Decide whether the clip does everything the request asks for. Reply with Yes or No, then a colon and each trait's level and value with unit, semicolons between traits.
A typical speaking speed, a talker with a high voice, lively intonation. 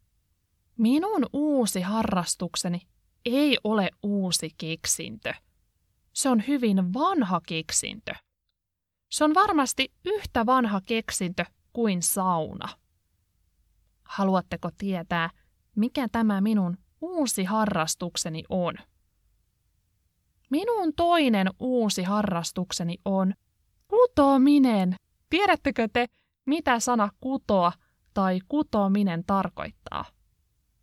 No: slow, 80 wpm; high, 200 Hz; wide, 6.7 semitones